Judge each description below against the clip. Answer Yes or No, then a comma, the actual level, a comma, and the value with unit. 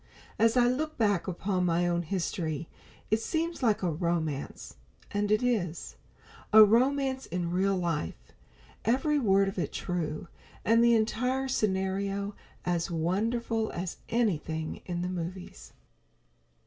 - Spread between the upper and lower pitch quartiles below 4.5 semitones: No, average, 4.9 semitones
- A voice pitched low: No, high, 195 Hz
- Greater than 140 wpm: No, slow, 135 wpm